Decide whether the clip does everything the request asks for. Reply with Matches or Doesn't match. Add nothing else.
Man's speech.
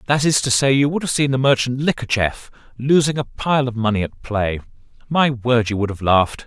Matches